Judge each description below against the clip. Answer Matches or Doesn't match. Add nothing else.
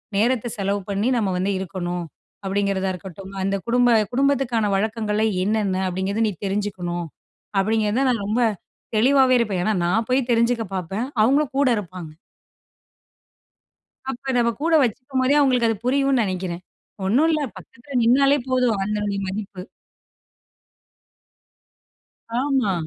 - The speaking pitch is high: Matches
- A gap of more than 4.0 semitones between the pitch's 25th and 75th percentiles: Matches